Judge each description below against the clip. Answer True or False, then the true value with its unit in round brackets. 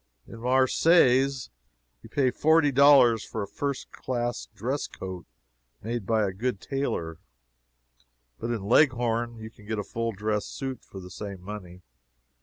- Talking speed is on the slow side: False (150 wpm)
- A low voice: True (115 Hz)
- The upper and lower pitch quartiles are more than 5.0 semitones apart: False (4.1 semitones)